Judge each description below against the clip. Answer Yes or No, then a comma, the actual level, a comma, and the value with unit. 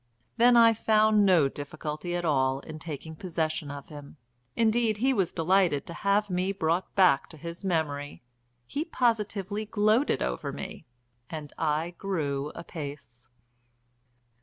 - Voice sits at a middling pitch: Yes, medium, 170 Hz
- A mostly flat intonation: No, wide, 5.6 semitones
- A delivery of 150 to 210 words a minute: No, slow, 135 wpm